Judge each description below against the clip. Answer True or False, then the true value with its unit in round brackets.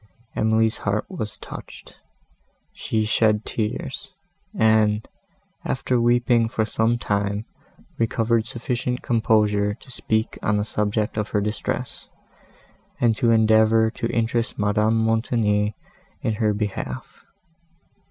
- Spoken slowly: True (115 wpm)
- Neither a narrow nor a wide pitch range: False (1.5 semitones)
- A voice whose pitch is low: True (110 Hz)